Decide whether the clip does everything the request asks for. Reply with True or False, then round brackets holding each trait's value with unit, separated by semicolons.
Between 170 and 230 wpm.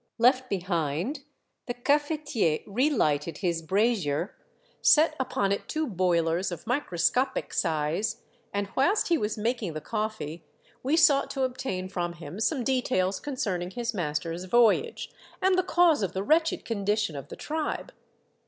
False (145 wpm)